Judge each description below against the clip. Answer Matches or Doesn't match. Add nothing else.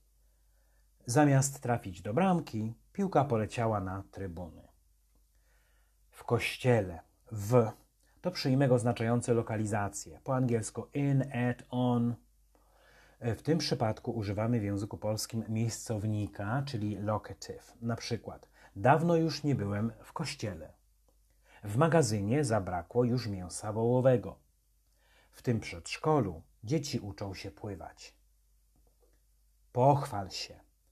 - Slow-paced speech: Matches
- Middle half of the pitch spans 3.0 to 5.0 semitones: Matches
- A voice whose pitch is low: Matches